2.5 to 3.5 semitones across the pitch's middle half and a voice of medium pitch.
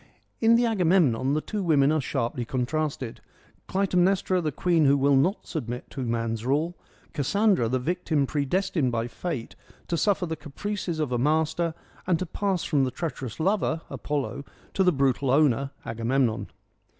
No: wide, 5.5 semitones; medium, 150 Hz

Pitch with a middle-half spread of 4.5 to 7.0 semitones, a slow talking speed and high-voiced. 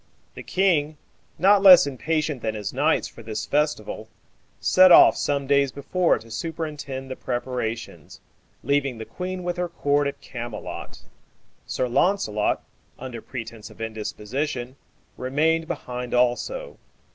No: average, 5.2 semitones; slow, 130 wpm; medium, 140 Hz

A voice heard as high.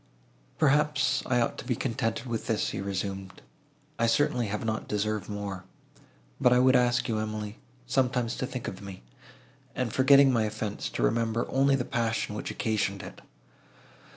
No: low, 115 Hz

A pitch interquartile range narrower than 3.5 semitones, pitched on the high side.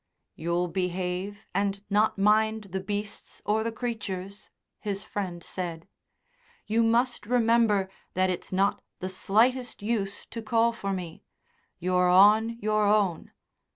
Yes: average, 2.9 semitones; high, 205 Hz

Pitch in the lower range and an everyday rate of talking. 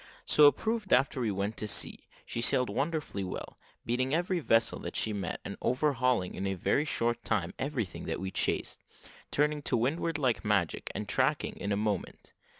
Yes: low, 125 Hz; average, 185 wpm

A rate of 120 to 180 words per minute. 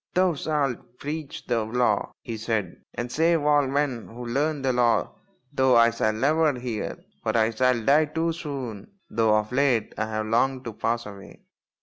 No: average, 190 wpm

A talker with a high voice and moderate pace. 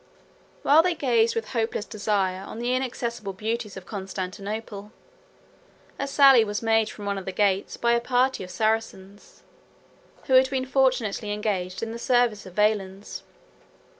Yes: high, 220 Hz; average, 160 wpm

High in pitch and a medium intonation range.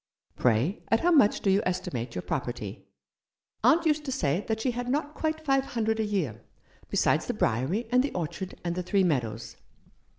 No: high, 210 Hz; wide, 8.4 semitones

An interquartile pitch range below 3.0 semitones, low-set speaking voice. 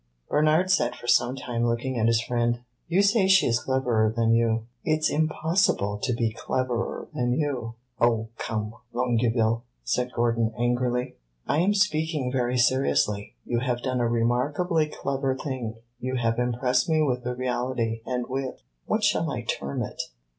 Yes: narrow, 2.5 semitones; low, 125 Hz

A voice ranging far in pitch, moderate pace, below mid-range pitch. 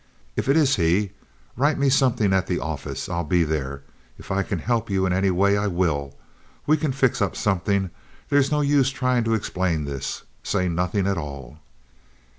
Yes: wide, 6.4 semitones; average, 190 wpm; very low, 95 Hz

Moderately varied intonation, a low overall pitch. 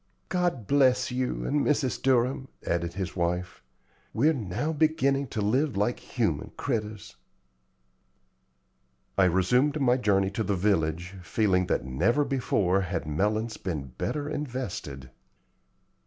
No: wide, 6.6 semitones; low, 110 Hz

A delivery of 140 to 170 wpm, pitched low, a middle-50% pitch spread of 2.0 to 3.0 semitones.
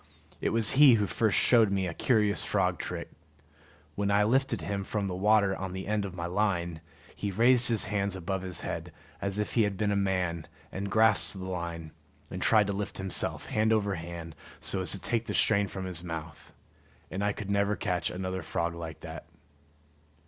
No: average, 200 wpm; low, 100 Hz; average, 2.7 semitones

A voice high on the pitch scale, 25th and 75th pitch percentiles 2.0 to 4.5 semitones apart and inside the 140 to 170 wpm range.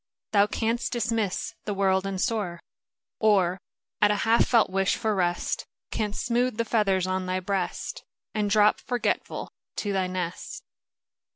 Yes: high, 205 Hz; average, 3.0 semitones; average, 150 wpm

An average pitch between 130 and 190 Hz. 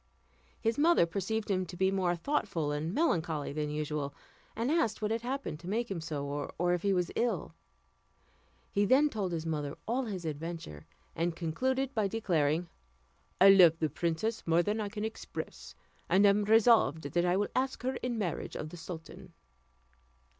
Yes: medium, 185 Hz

